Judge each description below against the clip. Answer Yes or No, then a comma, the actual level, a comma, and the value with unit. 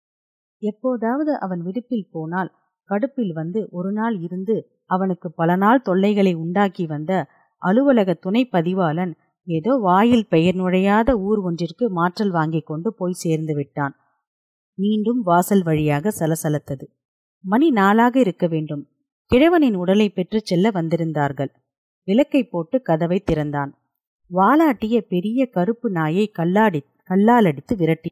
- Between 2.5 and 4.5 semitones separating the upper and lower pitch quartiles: No, average, 5.1 semitones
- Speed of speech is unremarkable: Yes, average, 115 wpm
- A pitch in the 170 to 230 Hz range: Yes, medium, 185 Hz